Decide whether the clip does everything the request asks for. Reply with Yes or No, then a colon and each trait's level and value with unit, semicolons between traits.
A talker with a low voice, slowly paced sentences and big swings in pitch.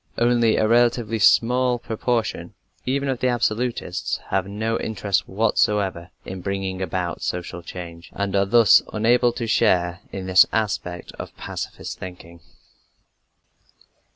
No: low, 105 Hz; slow, 125 wpm; average, 4.1 semitones